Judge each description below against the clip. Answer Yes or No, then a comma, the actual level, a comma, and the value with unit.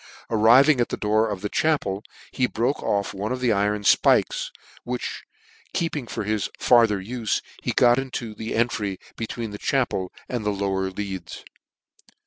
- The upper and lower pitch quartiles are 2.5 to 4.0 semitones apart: Yes, average, 3.5 semitones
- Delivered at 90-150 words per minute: No, average, 160 wpm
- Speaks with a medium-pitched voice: No, low, 110 Hz